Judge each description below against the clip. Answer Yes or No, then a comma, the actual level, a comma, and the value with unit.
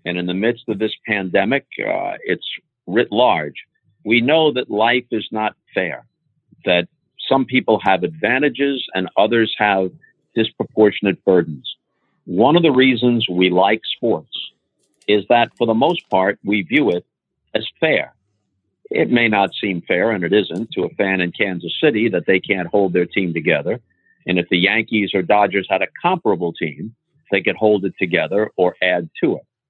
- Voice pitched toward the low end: Yes, low, 105 Hz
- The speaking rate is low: No, average, 175 wpm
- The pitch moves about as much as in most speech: Yes, average, 3.9 semitones